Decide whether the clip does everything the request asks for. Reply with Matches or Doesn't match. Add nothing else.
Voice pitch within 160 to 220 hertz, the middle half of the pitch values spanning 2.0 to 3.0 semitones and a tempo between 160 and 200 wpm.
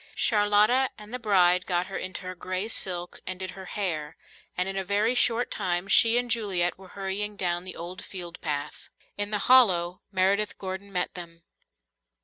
Matches